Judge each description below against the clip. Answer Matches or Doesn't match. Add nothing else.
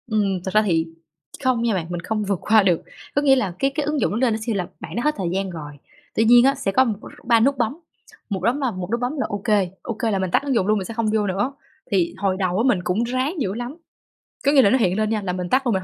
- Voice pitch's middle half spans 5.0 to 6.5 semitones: Doesn't match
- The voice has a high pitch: Matches